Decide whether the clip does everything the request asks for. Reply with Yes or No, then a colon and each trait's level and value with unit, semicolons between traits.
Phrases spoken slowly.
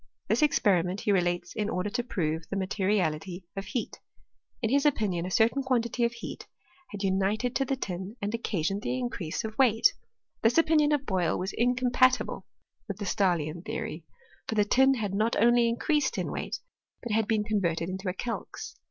No: average, 185 wpm